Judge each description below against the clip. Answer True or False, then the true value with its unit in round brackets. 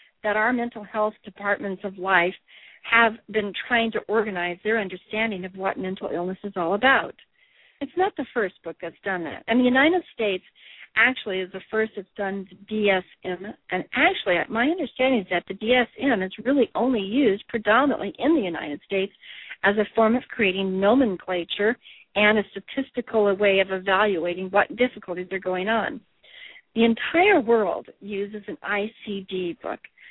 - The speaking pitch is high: True (210 Hz)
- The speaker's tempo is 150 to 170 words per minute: True (165 wpm)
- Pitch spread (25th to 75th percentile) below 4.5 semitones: True (4.1 semitones)